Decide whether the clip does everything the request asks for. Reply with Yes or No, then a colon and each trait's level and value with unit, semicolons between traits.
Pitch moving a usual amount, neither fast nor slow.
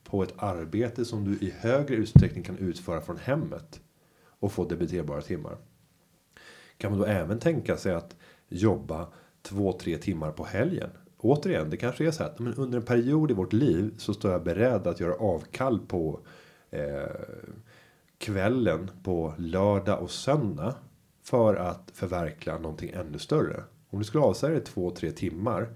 Yes: average, 5.0 semitones; average, 160 wpm